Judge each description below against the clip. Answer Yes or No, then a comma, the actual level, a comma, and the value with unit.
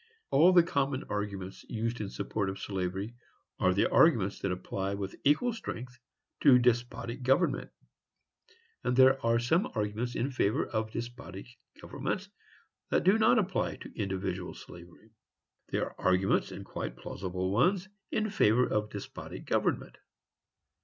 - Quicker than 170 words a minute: No, average, 140 wpm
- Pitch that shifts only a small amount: No, wide, 5.5 semitones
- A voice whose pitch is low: Yes, low, 115 Hz